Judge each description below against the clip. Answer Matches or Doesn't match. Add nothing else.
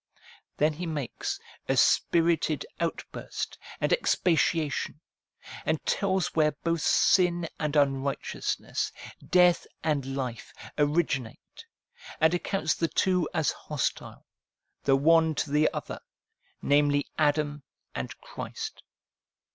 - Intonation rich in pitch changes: Doesn't match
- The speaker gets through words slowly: Matches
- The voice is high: Doesn't match